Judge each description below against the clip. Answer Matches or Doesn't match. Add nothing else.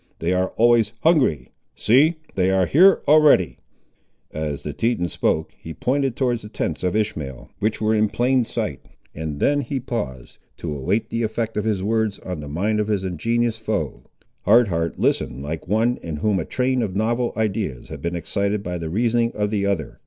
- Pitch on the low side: Matches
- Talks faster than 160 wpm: Matches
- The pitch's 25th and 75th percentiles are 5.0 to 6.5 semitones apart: Matches